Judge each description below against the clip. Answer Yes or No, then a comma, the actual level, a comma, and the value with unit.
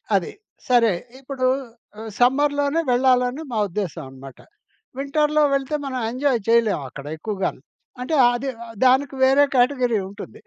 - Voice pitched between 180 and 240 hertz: No, very high, 250 Hz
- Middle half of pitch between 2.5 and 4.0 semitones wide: No, average, 4.4 semitones